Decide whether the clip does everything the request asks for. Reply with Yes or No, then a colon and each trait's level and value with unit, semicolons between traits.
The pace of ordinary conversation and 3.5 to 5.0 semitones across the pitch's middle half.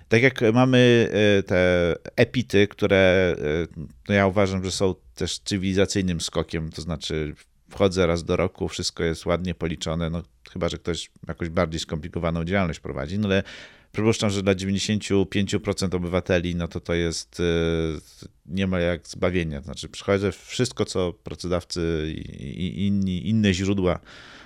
No: average, 140 wpm; average, 3.1 semitones